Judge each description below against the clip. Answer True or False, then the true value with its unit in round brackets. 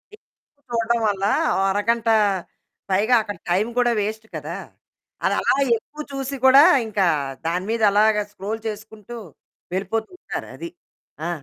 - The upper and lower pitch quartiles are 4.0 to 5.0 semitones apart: False (2.7 semitones)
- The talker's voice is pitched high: True (220 Hz)